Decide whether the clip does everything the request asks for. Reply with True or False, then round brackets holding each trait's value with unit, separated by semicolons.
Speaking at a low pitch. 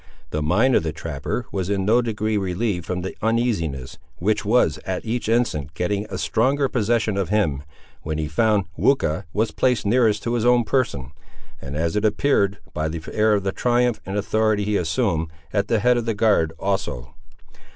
True (105 Hz)